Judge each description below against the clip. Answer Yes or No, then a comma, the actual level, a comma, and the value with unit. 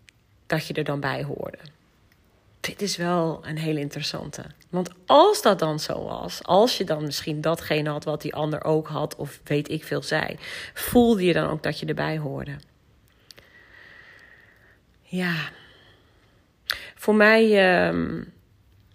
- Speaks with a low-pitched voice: No, medium, 155 Hz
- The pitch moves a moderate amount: Yes, average, 4.0 semitones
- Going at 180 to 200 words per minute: No, average, 145 wpm